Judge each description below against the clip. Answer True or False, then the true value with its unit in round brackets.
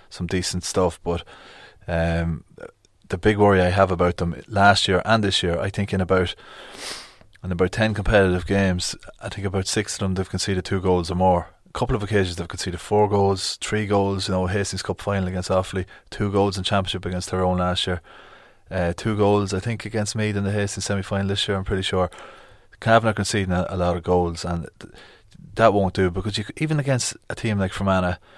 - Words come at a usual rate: False (210 wpm)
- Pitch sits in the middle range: False (95 Hz)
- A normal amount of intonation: False (2.0 semitones)